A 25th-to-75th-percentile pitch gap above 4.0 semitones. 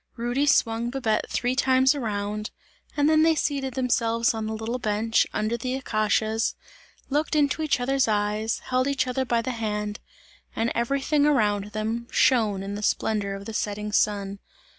No: average, 3.7 semitones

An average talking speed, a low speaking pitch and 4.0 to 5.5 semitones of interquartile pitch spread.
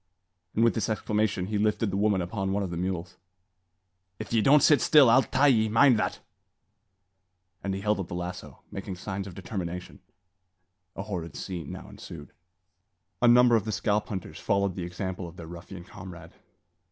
No: average, 185 wpm; low, 100 Hz; average, 3.3 semitones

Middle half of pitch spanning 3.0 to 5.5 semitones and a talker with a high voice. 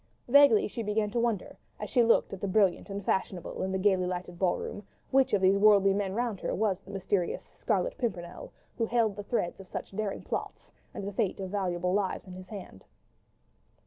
No: narrow, 2.6 semitones; high, 200 Hz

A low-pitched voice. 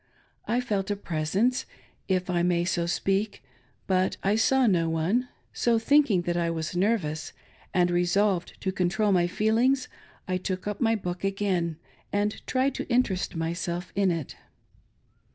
No: high, 190 Hz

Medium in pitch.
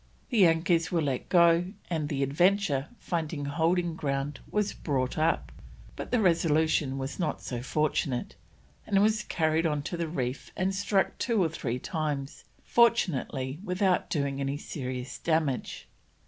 Yes: medium, 160 Hz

